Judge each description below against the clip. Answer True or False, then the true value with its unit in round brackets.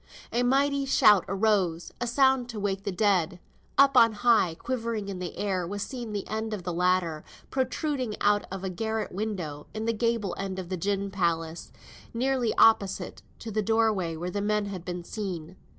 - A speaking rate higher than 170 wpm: True (185 wpm)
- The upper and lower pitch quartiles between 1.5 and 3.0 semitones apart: False (3.9 semitones)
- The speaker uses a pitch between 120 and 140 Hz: False (205 Hz)